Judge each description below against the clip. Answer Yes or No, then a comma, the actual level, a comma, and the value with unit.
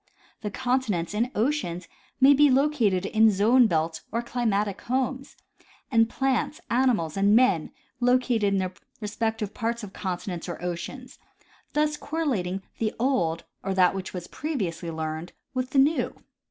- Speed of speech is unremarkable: Yes, average, 145 wpm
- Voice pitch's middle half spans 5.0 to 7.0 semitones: Yes, wide, 5.6 semitones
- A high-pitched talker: Yes, high, 220 Hz